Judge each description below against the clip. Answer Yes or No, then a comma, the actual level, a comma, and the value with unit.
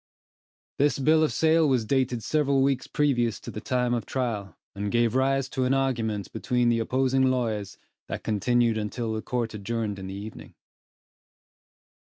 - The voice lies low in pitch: Yes, low, 120 Hz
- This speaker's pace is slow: No, average, 165 wpm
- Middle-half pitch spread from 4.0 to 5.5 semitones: No, average, 3.4 semitones